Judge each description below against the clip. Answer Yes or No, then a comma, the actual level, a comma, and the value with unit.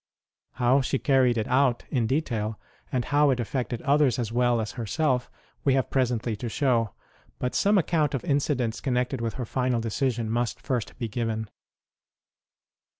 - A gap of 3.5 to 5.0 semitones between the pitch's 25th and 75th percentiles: No, average, 2.7 semitones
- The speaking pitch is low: Yes, low, 125 Hz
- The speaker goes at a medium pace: Yes, average, 160 wpm